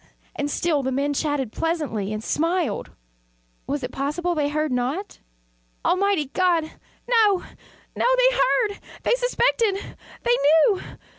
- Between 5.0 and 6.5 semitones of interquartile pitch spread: Yes, wide, 5.4 semitones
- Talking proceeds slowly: Yes, slow, 130 wpm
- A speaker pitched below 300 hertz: No, very high, 315 Hz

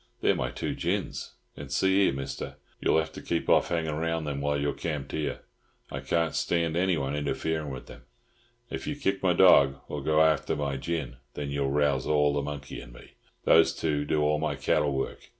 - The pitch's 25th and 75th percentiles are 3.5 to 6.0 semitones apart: No, narrow, 2.6 semitones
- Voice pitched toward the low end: Yes, very low, 75 Hz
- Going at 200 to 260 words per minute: Yes, fast, 205 wpm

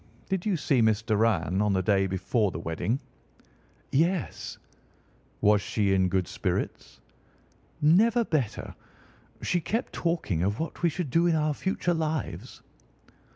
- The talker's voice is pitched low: Yes, low, 125 Hz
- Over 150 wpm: No, average, 140 wpm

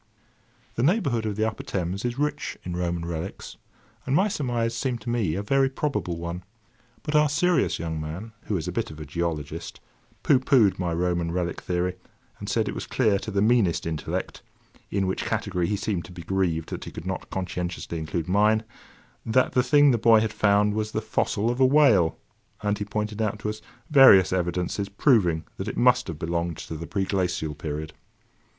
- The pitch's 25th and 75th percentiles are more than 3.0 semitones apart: Yes, average, 5.1 semitones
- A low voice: Yes, low, 100 Hz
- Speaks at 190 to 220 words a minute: Yes, average, 195 wpm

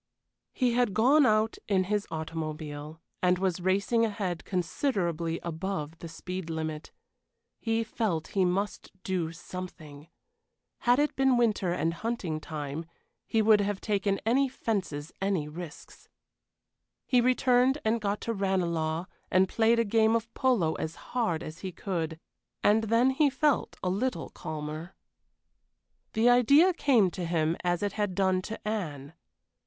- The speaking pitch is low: No, high, 190 Hz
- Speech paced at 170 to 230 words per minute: No, average, 145 wpm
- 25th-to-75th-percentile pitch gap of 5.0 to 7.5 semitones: Yes, wide, 5.5 semitones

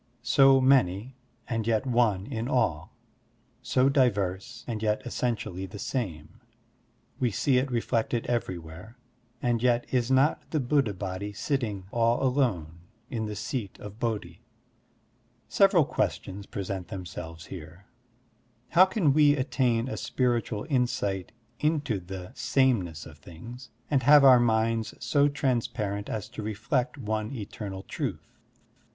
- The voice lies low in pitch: Yes, low, 115 Hz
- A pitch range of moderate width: Yes, average, 4.7 semitones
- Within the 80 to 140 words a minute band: Yes, slow, 135 wpm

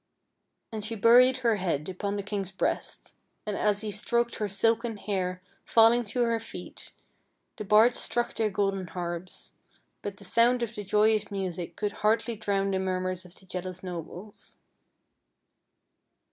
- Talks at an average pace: Yes, average, 155 wpm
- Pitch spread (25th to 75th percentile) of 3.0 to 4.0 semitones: Yes, average, 3.3 semitones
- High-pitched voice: Yes, high, 205 Hz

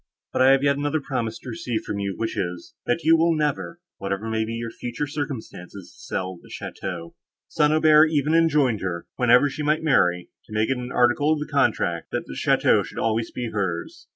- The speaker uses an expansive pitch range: Yes, wide, 6.6 semitones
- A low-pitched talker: Yes, low, 125 Hz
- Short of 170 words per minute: No, fast, 205 wpm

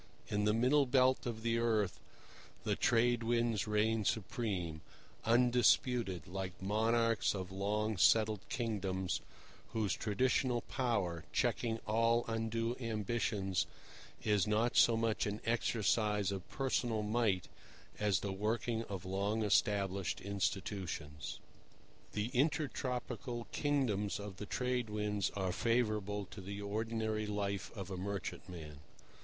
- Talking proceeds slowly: Yes, slow, 120 wpm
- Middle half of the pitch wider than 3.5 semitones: No, average, 2.8 semitones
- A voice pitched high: No, low, 105 Hz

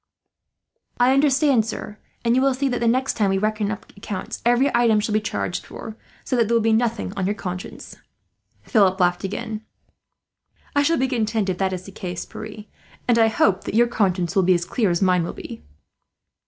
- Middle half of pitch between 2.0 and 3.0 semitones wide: No, average, 3.8 semitones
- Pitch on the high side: Yes, high, 215 Hz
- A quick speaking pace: Yes, fast, 210 wpm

